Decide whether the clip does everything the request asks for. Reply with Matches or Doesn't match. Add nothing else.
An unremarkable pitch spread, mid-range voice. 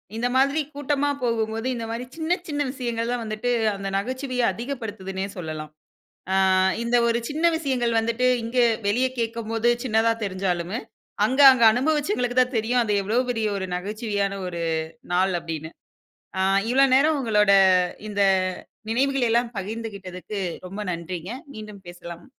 Doesn't match